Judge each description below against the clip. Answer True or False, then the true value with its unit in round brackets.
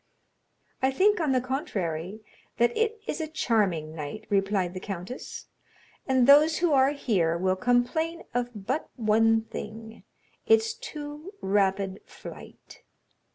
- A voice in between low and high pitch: False (235 Hz)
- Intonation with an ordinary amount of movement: False (7.2 semitones)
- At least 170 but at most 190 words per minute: False (140 wpm)